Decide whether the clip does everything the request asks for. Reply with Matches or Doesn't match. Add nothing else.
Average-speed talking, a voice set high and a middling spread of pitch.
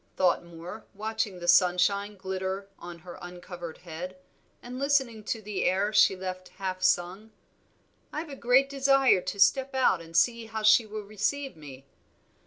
Matches